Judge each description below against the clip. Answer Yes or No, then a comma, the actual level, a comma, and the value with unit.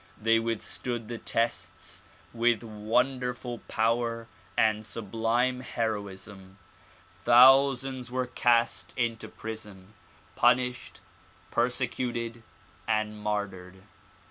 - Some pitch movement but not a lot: No, narrow, 2.3 semitones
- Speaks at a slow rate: Yes, slow, 80 wpm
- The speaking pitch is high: No, low, 115 Hz